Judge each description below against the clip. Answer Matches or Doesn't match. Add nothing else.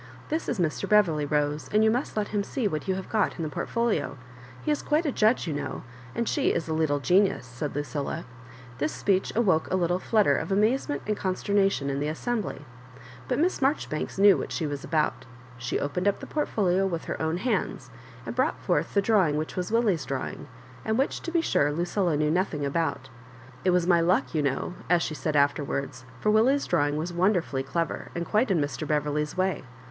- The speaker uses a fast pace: Matches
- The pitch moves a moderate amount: Doesn't match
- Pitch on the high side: Doesn't match